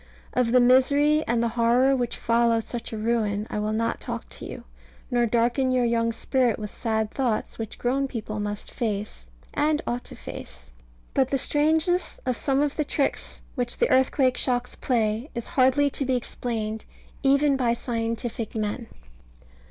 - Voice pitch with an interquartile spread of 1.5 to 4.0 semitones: Yes, average, 2.8 semitones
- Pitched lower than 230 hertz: No, high, 240 Hz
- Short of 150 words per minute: No, average, 170 wpm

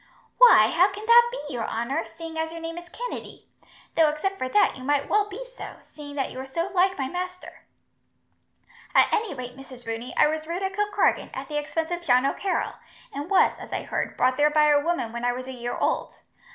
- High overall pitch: Yes, very high, 310 Hz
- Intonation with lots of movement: Yes, wide, 5.8 semitones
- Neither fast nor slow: No, fast, 225 wpm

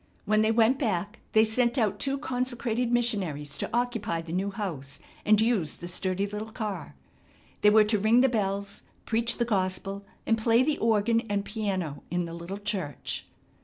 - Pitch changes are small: No, average, 3.6 semitones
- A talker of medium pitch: No, high, 210 Hz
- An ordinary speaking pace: Yes, average, 175 wpm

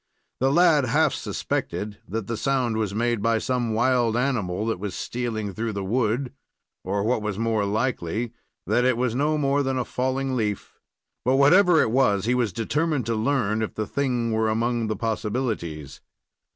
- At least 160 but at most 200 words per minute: Yes, average, 180 wpm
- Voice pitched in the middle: No, low, 115 Hz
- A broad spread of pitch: No, average, 3.2 semitones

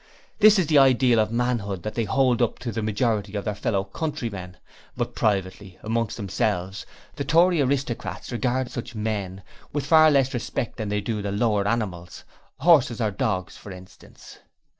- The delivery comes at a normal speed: Yes, average, 170 wpm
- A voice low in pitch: Yes, low, 110 Hz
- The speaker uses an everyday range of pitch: Yes, average, 4.2 semitones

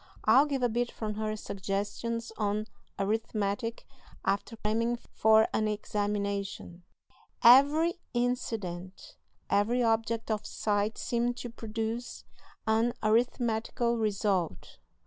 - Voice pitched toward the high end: Yes, high, 220 Hz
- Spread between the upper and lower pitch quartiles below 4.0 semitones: Yes, narrow, 2.4 semitones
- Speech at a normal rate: No, slow, 105 wpm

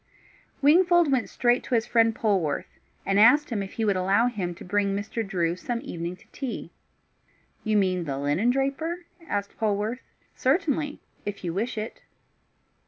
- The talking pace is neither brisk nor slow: Yes, average, 165 wpm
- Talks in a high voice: Yes, high, 220 Hz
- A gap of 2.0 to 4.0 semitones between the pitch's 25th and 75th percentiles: No, average, 4.9 semitones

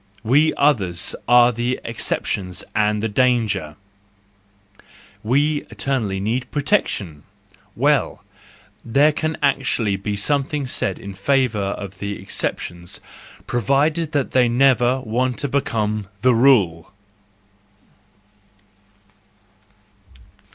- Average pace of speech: No, slow, 100 wpm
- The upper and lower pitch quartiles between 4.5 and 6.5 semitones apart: Yes, average, 5.1 semitones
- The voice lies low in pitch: Yes, low, 120 Hz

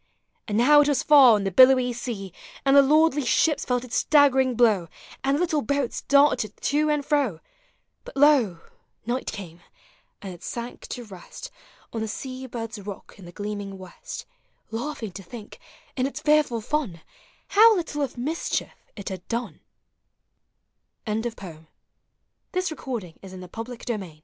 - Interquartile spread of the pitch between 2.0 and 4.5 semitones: No, wide, 5.6 semitones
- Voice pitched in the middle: No, very high, 250 Hz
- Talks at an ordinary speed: Yes, average, 145 wpm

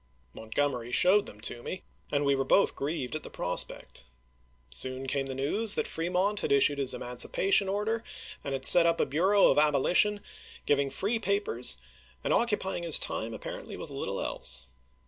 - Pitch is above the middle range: No, medium, 150 Hz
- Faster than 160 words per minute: Yes, average, 170 wpm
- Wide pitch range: Yes, wide, 6.8 semitones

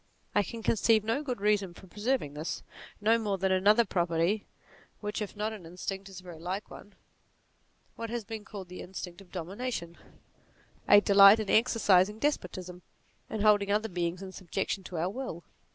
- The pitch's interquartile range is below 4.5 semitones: Yes, average, 3.0 semitones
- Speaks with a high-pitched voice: Yes, high, 200 Hz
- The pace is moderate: Yes, average, 180 wpm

